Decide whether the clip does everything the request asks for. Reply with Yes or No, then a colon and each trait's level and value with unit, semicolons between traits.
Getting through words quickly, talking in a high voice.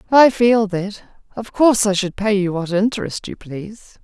No: average, 195 wpm; high, 205 Hz